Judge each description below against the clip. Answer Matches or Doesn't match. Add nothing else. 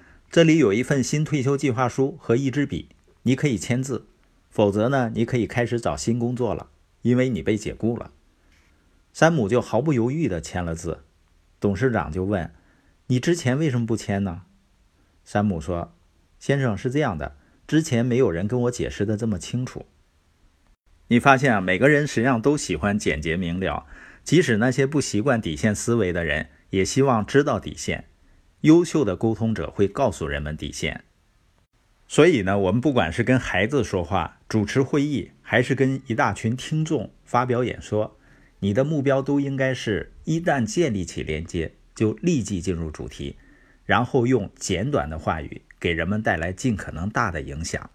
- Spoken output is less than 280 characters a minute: Matches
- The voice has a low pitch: Matches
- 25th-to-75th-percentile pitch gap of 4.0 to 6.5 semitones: Doesn't match